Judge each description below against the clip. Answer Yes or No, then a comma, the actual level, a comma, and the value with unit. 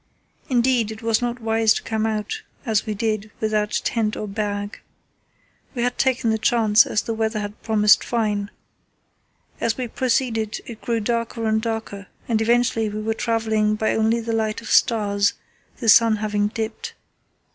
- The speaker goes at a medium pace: Yes, average, 170 wpm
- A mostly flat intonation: Yes, narrow, 1.4 semitones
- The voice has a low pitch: No, high, 220 Hz